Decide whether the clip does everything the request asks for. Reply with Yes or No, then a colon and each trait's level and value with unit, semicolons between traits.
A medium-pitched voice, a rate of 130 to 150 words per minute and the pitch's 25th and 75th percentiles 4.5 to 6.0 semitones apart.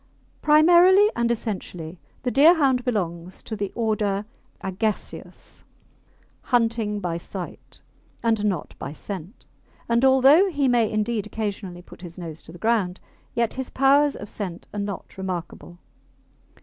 No: high, 215 Hz; slow, 135 wpm; average, 5.3 semitones